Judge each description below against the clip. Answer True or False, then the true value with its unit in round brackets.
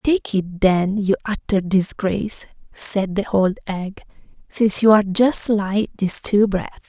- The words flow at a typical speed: True (155 wpm)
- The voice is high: True (200 Hz)